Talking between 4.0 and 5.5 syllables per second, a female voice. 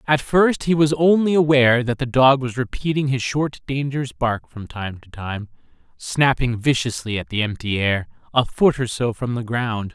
No: 4.8 syllables/s; male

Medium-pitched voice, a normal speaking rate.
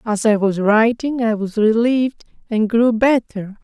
No: high, 225 Hz; average, 165 wpm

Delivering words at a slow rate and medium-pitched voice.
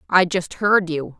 No: average, 200 wpm; medium, 175 Hz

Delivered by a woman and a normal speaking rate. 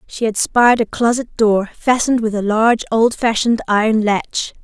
Yes: female; average, 170 wpm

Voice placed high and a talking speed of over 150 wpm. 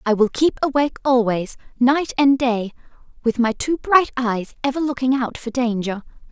Yes: very high, 250 Hz; average, 170 wpm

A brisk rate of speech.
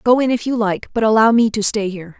Yes: fast, 300 wpm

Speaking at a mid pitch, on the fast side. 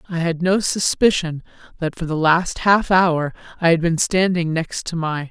No: medium, 170 Hz; average, 190 wpm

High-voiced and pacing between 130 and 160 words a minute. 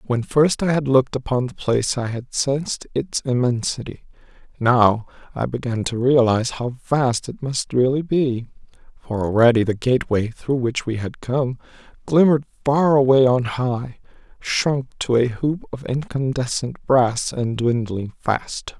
No: low, 125 Hz; average, 150 wpm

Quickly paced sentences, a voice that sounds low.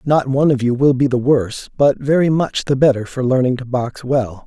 Yes: fast, 240 wpm; low, 130 Hz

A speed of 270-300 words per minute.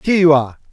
No: fast, 250 wpm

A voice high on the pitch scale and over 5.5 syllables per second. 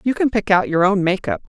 Yes: high, 205 Hz; 6.0 syllables/s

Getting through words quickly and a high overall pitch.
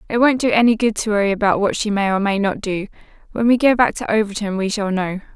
Yes: fast, 270 wpm; high, 210 Hz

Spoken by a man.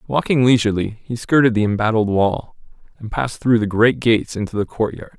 Yes: male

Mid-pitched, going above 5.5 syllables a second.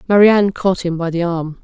Yes: medium, 180 Hz; 6.2 syllables/s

